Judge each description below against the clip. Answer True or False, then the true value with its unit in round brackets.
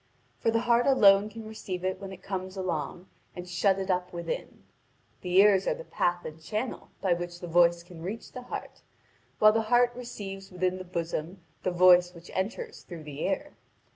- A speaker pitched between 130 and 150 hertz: False (185 Hz)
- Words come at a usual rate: True (195 wpm)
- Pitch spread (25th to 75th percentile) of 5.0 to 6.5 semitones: False (3.3 semitones)